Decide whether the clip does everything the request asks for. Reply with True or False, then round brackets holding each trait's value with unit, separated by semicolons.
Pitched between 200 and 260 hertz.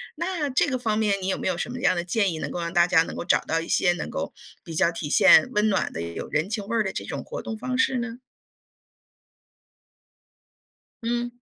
True (205 Hz)